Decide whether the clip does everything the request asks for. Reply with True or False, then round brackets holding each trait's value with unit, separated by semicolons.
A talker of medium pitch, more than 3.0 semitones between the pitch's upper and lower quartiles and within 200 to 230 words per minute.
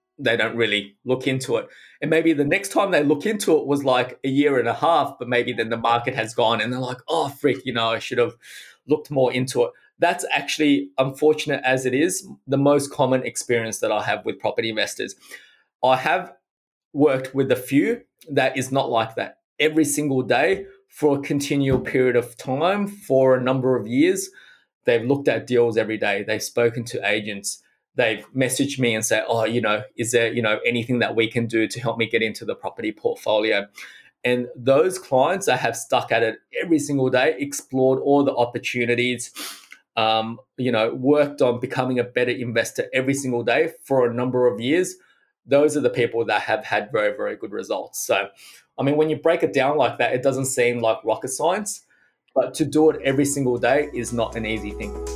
False (130 Hz; 3.8 semitones; 205 wpm)